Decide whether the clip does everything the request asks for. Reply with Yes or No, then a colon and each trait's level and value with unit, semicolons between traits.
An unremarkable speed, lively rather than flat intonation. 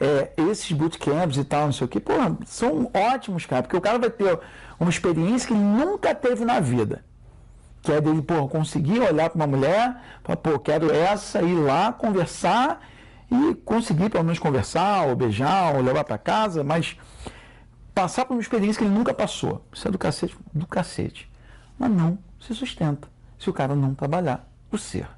No: fast, 190 wpm; wide, 6.7 semitones